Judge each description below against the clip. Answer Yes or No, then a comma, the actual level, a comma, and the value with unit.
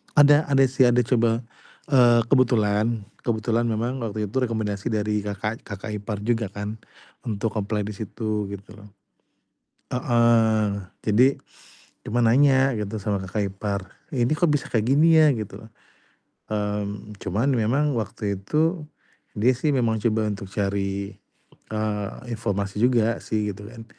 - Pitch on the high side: No, low, 110 Hz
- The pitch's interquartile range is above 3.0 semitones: No, average, 2.7 semitones